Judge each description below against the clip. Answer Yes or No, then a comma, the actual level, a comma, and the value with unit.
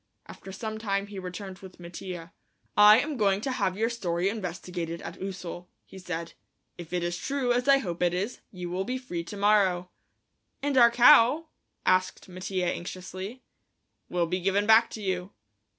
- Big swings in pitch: No, average, 3.7 semitones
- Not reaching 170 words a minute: No, average, 175 wpm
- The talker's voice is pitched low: No, high, 190 Hz